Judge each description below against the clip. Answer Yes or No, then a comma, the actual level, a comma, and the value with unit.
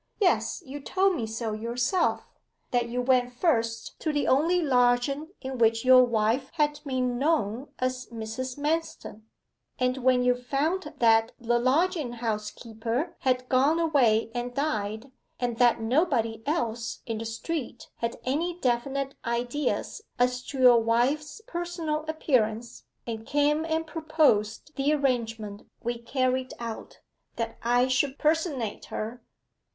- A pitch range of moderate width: Yes, average, 4.2 semitones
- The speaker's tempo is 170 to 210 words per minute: No, average, 140 wpm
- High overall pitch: Yes, very high, 255 Hz